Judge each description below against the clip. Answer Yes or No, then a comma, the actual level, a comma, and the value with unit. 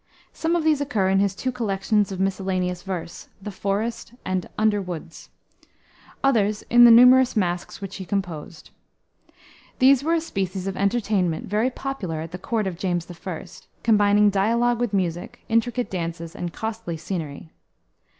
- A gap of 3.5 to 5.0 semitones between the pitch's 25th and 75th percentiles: Yes, average, 4.4 semitones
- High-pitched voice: Yes, high, 200 Hz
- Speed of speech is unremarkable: Yes, average, 150 wpm